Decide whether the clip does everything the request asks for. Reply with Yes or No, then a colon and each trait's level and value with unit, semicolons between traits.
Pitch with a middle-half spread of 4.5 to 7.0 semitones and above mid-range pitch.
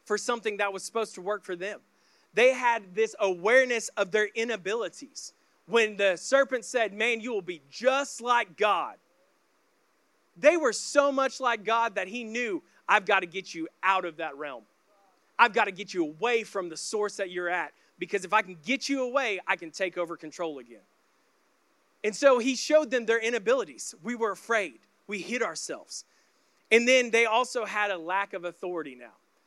No: average, 4.1 semitones; high, 215 Hz